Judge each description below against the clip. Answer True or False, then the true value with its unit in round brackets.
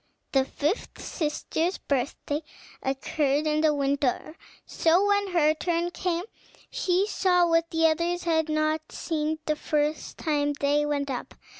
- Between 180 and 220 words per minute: False (140 wpm)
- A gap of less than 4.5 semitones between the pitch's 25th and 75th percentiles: True (2.6 semitones)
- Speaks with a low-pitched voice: False (310 Hz)